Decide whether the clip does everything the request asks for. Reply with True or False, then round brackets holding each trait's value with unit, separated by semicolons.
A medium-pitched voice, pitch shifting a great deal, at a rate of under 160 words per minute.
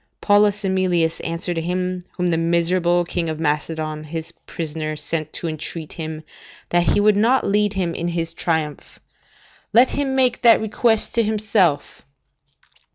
False (175 Hz; 4.1 semitones; 150 wpm)